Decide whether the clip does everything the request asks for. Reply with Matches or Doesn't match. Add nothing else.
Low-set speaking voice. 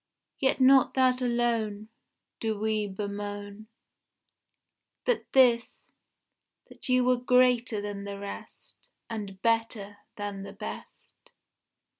Doesn't match